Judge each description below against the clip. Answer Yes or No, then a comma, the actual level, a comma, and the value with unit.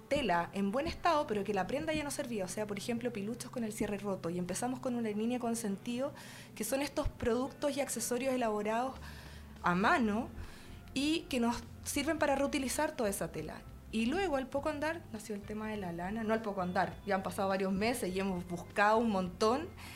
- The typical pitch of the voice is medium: No, high, 225 Hz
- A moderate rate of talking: No, fast, 215 wpm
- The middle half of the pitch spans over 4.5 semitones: Yes, average, 5.1 semitones